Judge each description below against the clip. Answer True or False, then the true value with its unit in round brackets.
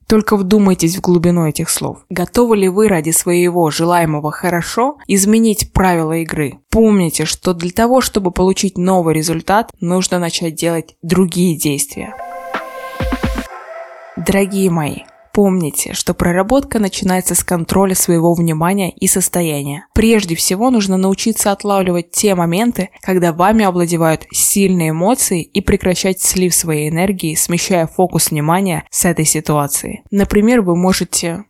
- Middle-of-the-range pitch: True (180 Hz)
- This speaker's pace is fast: False (130 wpm)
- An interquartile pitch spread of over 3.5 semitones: False (3.0 semitones)